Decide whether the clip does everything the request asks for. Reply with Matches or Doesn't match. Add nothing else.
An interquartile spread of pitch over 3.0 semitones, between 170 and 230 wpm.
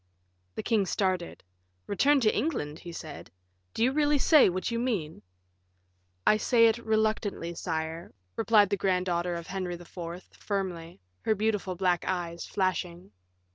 Doesn't match